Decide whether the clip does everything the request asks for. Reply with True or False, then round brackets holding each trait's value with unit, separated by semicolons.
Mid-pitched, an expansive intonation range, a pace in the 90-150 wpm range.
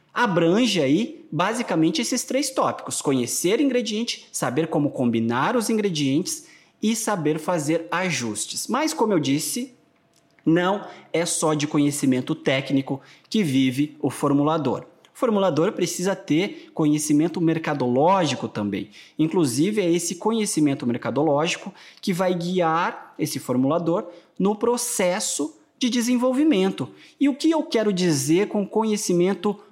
True (180 Hz; 6.7 semitones; 120 wpm)